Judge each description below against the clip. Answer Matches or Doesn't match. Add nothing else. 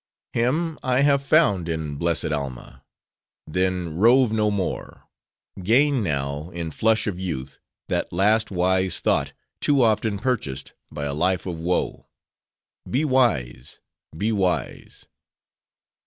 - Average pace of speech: Doesn't match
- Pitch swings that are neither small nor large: Doesn't match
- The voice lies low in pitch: Matches